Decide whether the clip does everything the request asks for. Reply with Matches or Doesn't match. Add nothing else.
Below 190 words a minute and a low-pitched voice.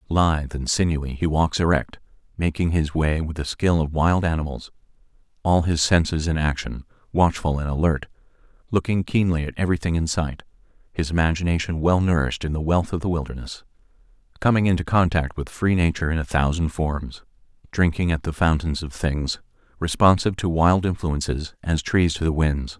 Matches